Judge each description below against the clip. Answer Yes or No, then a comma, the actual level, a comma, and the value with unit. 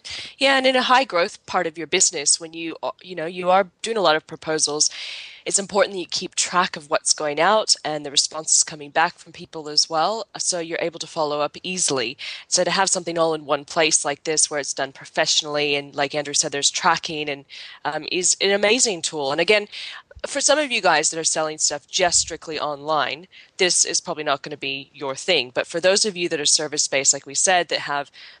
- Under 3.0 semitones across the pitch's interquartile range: No, average, 3.5 semitones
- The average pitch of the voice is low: No, medium, 160 Hz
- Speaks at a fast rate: Yes, fast, 230 wpm